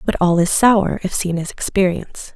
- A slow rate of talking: No, fast, 205 wpm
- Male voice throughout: No, female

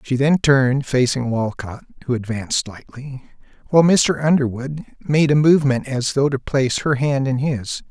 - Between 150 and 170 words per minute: Yes, average, 165 wpm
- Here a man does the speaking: Yes, male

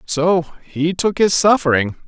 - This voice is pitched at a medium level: Yes, medium, 165 Hz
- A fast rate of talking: No, average, 145 wpm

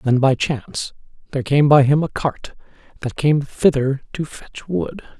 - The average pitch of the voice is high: No, medium, 140 Hz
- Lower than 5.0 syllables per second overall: Yes, 4.5 syllables/s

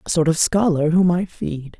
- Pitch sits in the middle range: Yes, medium, 170 Hz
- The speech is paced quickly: Yes, fast, 235 wpm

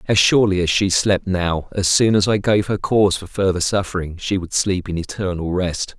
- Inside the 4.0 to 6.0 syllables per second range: Yes, 5.2 syllables/s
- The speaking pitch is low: Yes, very low, 95 Hz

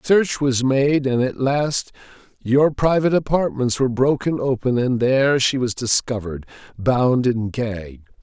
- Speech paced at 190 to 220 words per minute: No, average, 145 wpm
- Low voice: Yes, low, 130 Hz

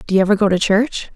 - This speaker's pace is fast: Yes, fast, 310 wpm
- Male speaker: No, female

